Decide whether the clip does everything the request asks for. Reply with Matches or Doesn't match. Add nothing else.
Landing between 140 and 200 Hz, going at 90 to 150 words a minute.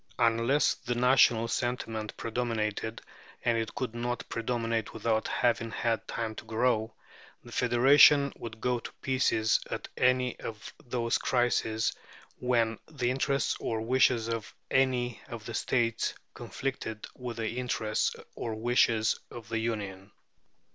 Doesn't match